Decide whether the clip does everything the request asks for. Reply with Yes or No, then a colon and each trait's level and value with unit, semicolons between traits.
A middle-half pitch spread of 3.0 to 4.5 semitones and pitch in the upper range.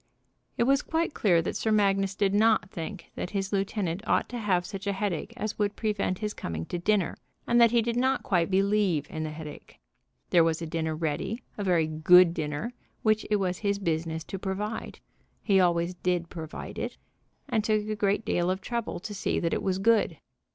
Yes: average, 3.9 semitones; high, 195 Hz